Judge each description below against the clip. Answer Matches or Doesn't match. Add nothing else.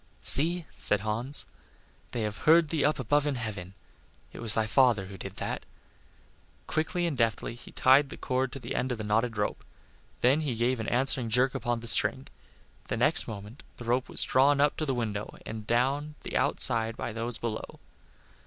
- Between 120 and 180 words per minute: Doesn't match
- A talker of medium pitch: Doesn't match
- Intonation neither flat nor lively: Matches